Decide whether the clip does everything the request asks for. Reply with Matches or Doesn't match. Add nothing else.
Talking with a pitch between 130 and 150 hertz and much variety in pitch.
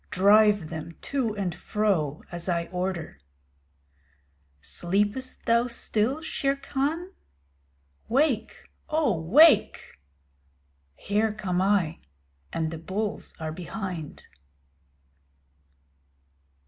Doesn't match